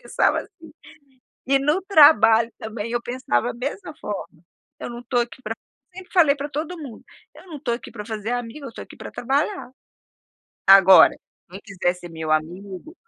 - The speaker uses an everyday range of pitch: No, wide, 6.6 semitones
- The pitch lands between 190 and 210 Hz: No, high, 240 Hz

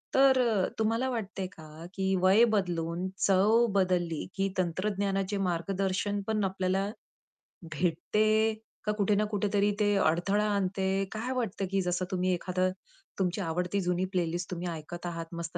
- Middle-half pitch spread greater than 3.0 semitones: No, average, 2.7 semitones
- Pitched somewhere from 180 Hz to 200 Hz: Yes, high, 190 Hz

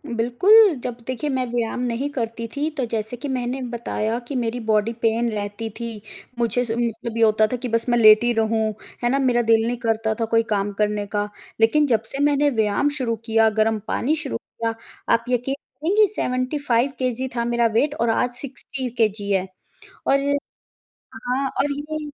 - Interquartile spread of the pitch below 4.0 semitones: Yes, average, 2.8 semitones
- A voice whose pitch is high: Yes, high, 235 Hz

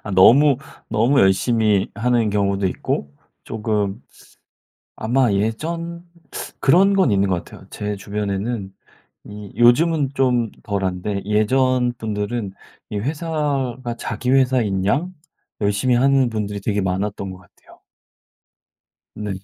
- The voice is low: Yes, low, 110 Hz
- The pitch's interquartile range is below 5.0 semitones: Yes, average, 4.4 semitones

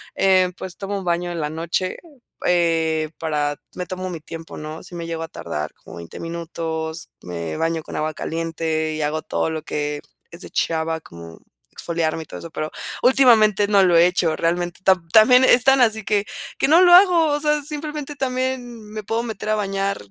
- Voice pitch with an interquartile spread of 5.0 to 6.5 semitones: Yes, average, 5.3 semitones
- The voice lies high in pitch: No, medium, 175 Hz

